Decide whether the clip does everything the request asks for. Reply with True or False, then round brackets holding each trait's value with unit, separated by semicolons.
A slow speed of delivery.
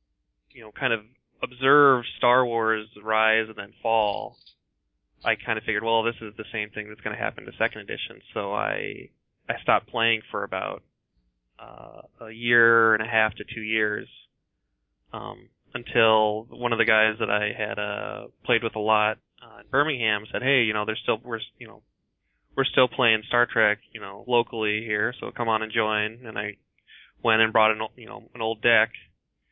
False (195 wpm)